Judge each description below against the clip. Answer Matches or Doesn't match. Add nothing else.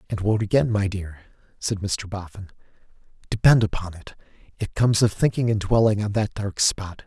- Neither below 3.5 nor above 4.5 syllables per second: Doesn't match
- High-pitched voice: Doesn't match